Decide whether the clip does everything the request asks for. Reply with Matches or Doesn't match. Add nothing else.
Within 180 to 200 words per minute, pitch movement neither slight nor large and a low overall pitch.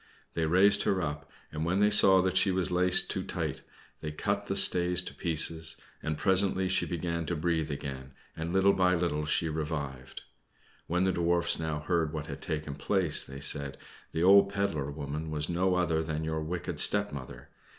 Matches